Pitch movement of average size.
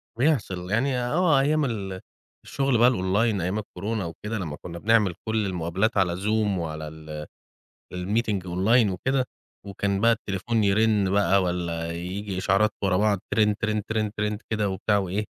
Yes: average, 3.3 semitones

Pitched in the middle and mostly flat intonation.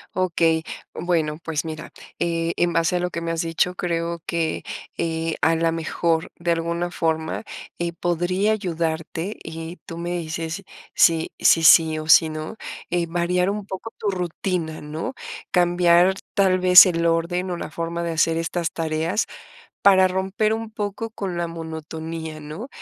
Yes: medium, 170 Hz; narrow, 1.8 semitones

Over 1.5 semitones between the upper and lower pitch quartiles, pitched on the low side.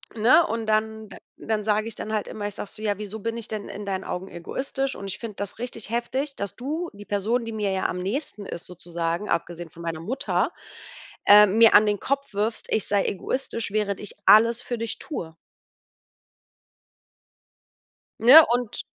No: narrow, 2.6 semitones; high, 215 Hz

